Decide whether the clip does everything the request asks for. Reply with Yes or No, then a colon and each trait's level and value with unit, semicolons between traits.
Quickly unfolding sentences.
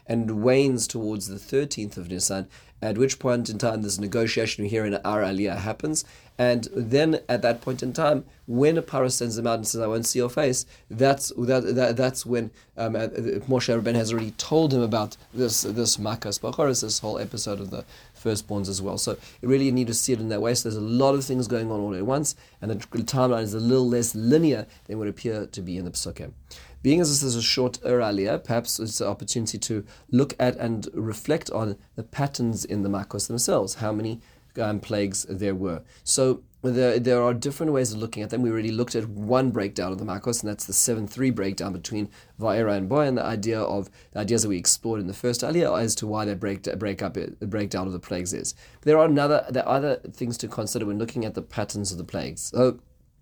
Yes: fast, 225 wpm